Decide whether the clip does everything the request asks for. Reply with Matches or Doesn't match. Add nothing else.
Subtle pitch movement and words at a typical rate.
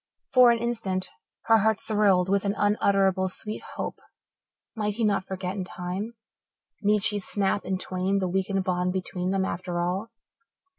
Matches